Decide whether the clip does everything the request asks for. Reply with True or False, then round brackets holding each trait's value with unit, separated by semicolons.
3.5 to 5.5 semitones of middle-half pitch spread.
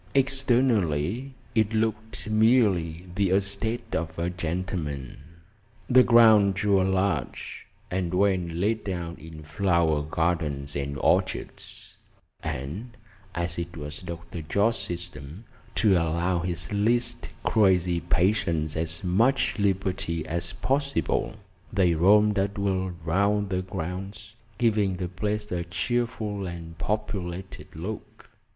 True (3.9 semitones)